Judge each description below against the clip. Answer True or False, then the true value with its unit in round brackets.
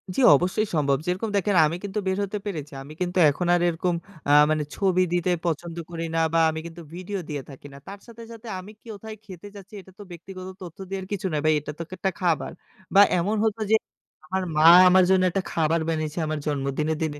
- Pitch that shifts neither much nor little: True (3.7 semitones)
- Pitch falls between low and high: True (175 Hz)